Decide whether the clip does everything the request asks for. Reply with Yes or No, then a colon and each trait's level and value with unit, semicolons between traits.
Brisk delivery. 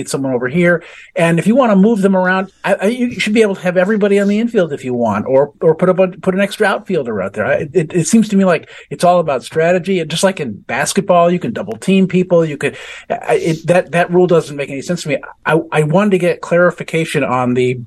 Yes: fast, 260 wpm